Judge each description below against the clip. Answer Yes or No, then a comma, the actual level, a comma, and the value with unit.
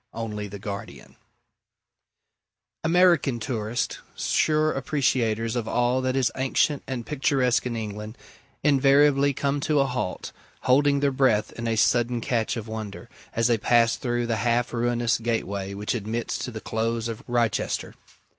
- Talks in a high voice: No, low, 120 Hz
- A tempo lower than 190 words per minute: Yes, average, 145 wpm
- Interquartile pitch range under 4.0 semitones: Yes, average, 3.2 semitones